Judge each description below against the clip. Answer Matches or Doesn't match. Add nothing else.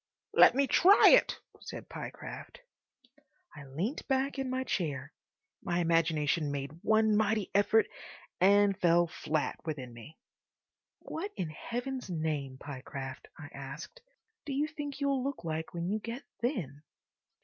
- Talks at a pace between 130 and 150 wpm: Matches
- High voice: Doesn't match